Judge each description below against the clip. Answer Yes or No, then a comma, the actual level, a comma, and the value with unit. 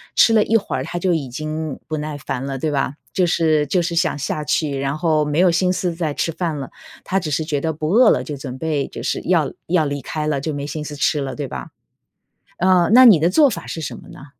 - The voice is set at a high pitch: No, medium, 155 Hz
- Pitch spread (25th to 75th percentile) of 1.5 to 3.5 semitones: Yes, average, 3.1 semitones